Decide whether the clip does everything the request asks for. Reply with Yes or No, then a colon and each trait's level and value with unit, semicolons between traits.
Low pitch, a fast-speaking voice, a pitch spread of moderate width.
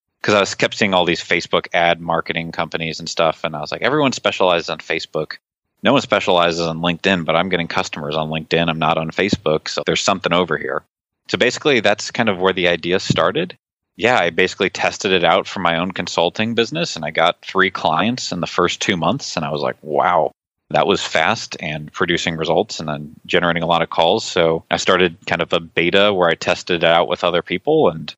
No: very low, 85 Hz; fast, 225 wpm; narrow, 1.9 semitones